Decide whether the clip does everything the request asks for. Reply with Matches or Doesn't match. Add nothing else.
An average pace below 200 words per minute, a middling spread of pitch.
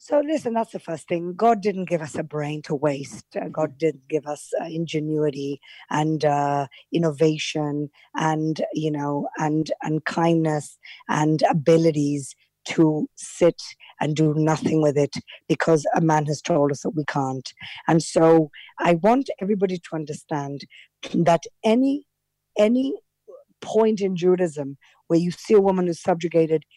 Matches